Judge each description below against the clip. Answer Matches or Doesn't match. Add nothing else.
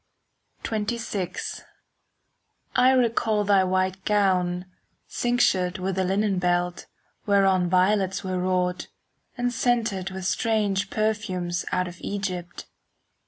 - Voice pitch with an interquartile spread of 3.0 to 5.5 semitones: Doesn't match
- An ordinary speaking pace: Doesn't match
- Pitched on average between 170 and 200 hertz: Matches